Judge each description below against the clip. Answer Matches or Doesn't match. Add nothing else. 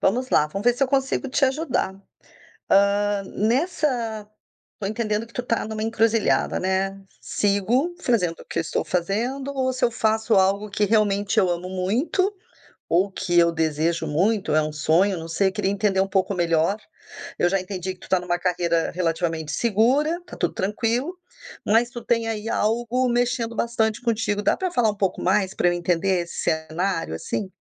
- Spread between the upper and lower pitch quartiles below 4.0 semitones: Doesn't match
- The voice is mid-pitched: Doesn't match